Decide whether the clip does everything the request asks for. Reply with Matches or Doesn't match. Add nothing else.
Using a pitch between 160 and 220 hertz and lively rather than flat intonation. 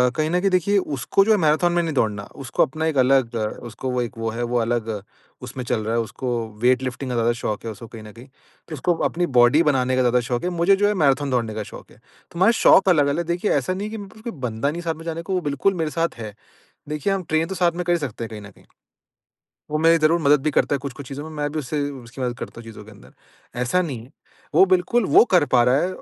Doesn't match